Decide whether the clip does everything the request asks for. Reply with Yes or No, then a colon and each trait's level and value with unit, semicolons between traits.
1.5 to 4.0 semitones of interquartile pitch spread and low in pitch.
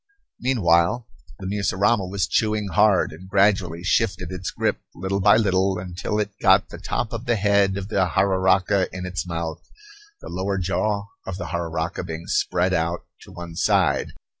Yes: narrow, 2.4 semitones; very low, 95 Hz